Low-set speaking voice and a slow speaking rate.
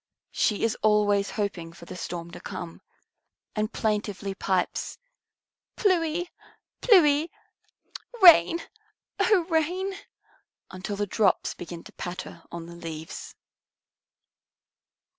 No: high, 205 Hz; slow, 105 wpm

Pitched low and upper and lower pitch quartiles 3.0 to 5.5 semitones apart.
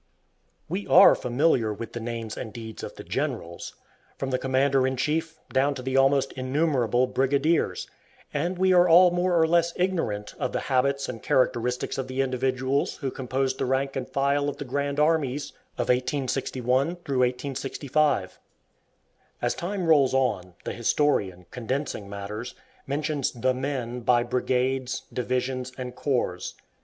No: low, 130 Hz; narrow, 2.6 semitones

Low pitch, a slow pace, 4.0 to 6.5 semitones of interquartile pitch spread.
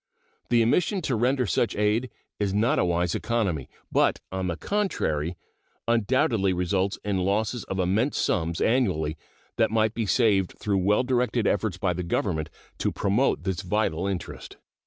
No: low, 100 Hz; average, 155 wpm; average, 4.3 semitones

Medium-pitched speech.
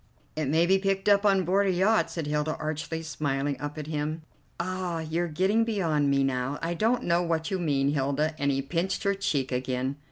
Yes: medium, 160 Hz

